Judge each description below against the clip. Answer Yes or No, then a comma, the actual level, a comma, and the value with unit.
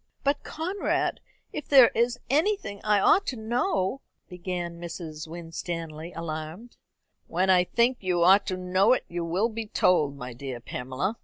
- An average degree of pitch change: No, wide, 5.9 semitones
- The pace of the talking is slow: No, average, 160 wpm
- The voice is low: No, medium, 185 Hz